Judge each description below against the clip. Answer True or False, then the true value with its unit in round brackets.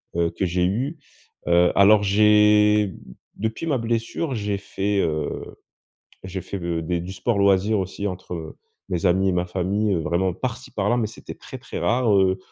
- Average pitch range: True (3.0 semitones)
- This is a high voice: False (100 Hz)